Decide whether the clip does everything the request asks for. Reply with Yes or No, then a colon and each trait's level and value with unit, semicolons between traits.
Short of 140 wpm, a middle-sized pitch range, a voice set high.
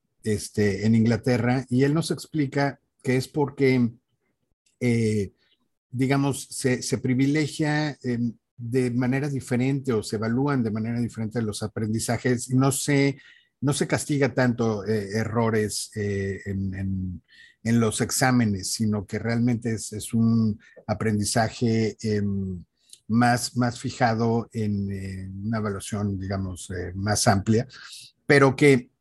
No: average, 130 wpm; average, 3.4 semitones; low, 115 Hz